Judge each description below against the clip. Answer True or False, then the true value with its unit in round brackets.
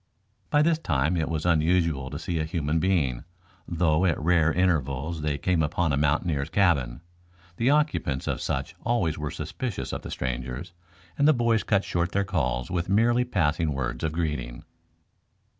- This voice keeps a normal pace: True (170 wpm)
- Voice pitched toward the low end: True (80 Hz)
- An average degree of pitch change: True (4.2 semitones)